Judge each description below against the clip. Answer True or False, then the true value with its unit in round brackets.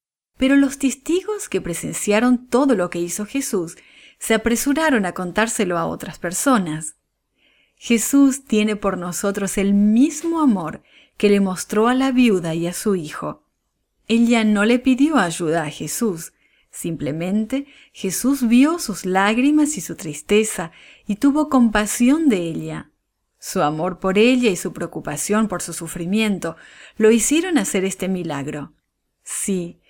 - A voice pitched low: False (210 Hz)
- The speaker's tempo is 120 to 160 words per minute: True (140 wpm)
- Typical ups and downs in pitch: False (6.1 semitones)